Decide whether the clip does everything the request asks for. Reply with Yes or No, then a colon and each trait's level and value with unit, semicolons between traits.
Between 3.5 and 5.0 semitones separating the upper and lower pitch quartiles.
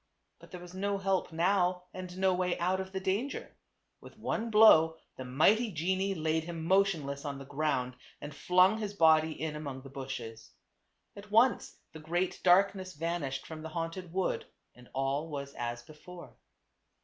Yes: average, 4.1 semitones